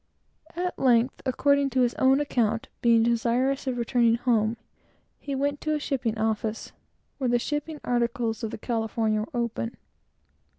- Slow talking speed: No, average, 155 wpm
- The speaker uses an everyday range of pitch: Yes, average, 3.0 semitones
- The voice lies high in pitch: Yes, high, 240 Hz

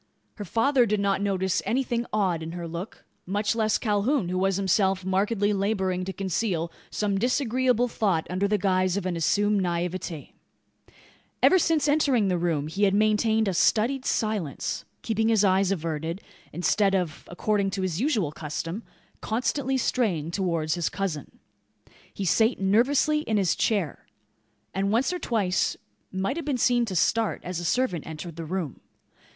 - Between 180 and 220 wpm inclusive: No, average, 160 wpm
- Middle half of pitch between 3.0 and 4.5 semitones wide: Yes, average, 3.9 semitones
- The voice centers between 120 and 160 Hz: No, high, 195 Hz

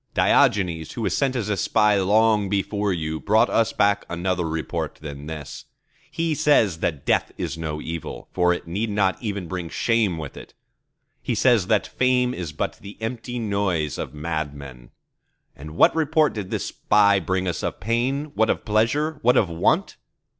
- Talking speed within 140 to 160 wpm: No, average, 175 wpm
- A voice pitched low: Yes, low, 100 Hz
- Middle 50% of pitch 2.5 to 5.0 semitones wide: No, wide, 5.4 semitones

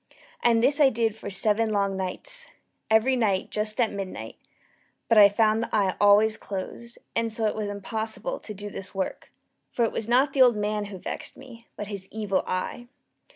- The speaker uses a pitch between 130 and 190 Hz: No, high, 215 Hz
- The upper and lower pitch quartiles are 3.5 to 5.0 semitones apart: No, narrow, 2.4 semitones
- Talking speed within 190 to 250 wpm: Yes, average, 195 wpm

